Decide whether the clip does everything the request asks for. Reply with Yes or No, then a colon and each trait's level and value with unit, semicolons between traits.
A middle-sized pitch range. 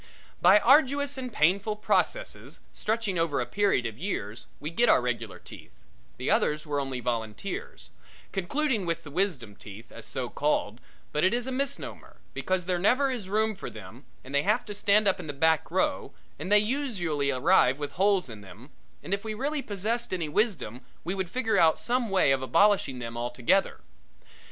No: wide, 8.2 semitones